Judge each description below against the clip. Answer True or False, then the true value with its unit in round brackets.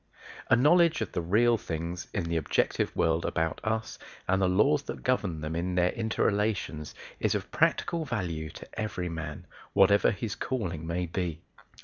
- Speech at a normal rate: True (170 wpm)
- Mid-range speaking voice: False (90 Hz)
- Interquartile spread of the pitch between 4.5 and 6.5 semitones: True (5.1 semitones)